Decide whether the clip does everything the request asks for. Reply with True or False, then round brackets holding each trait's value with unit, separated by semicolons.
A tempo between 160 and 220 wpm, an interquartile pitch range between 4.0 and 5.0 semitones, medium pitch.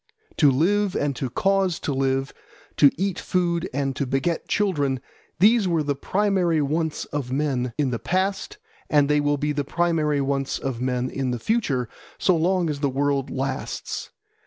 True (175 wpm; 4.5 semitones; 145 Hz)